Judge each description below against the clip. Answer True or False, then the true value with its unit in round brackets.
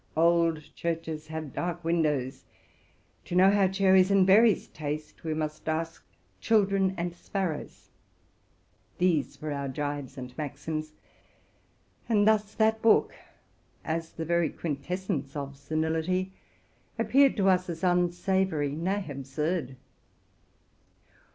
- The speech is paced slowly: True (120 wpm)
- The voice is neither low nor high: True (165 Hz)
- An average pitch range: True (3.8 semitones)